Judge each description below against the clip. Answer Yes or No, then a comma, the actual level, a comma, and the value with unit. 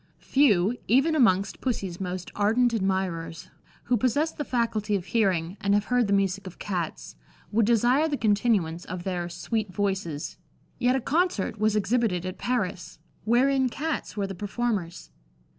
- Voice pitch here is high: Yes, high, 205 Hz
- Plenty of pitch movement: No, average, 4.9 semitones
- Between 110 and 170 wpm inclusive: Yes, average, 155 wpm